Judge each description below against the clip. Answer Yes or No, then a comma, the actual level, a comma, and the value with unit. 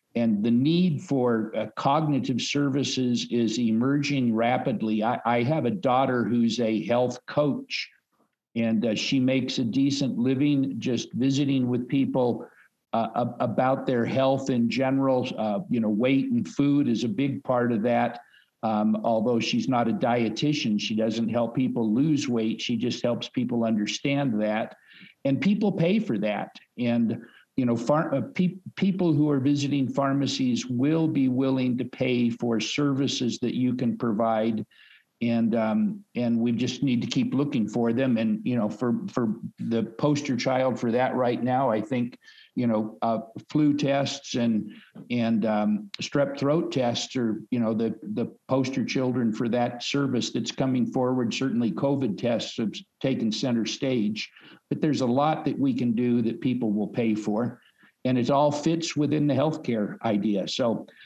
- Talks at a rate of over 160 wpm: Yes, average, 170 wpm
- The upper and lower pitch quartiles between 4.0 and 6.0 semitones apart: No, average, 3.3 semitones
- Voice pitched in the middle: No, low, 125 Hz